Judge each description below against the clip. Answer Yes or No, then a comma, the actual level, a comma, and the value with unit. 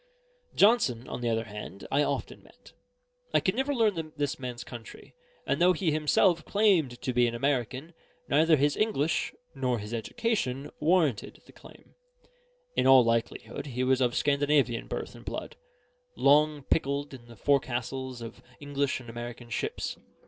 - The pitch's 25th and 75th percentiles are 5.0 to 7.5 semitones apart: No, average, 4.3 semitones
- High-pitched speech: No, low, 135 Hz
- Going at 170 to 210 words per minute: No, average, 155 wpm